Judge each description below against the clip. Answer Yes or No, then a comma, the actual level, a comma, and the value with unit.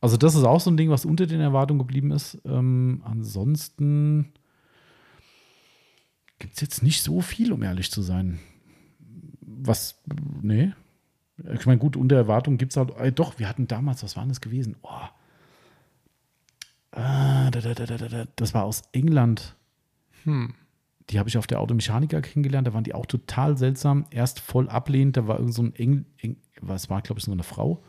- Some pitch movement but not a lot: Yes, average, 4.0 semitones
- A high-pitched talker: No, low, 130 Hz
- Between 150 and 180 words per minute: Yes, average, 170 wpm